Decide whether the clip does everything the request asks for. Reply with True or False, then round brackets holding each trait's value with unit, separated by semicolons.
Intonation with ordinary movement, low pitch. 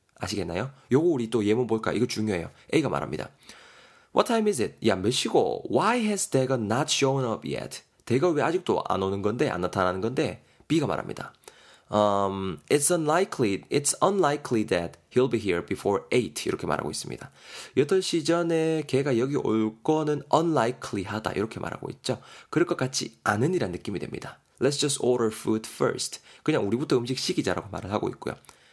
False (6.5 semitones; 130 Hz)